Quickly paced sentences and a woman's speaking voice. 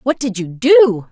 Yes: fast, 215 wpm; female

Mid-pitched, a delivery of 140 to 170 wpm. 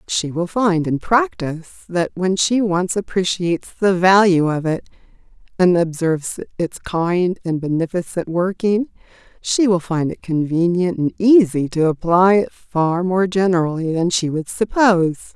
Yes: medium, 180 Hz; average, 150 wpm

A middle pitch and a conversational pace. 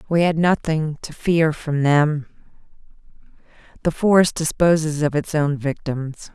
No: medium, 155 Hz; slow, 130 wpm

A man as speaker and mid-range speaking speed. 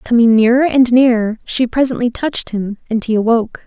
No: female; average, 180 wpm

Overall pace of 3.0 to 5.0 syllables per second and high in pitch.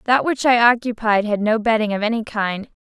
No: 5.4 syllables/s; high, 220 Hz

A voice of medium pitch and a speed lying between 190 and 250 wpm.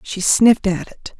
No: high, 200 Hz; average, 200 wpm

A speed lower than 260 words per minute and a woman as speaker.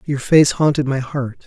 No: fast, 205 wpm; male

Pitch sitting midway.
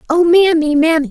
No: very high, 320 Hz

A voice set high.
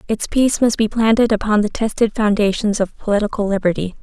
Yes: high, 215 Hz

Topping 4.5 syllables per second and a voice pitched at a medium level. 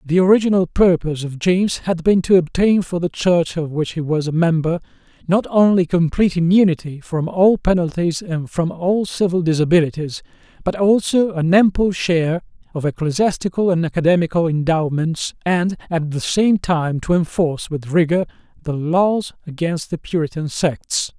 Yes: 5.0 syllables/s; medium, 170 Hz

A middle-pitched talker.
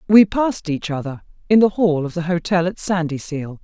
Yes: medium, 175 Hz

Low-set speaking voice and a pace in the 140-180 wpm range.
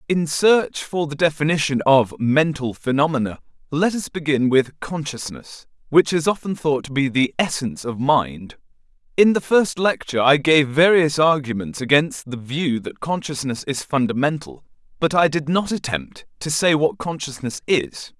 No: medium, 145 Hz; average, 160 wpm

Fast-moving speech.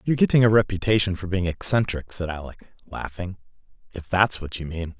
No: average, 180 wpm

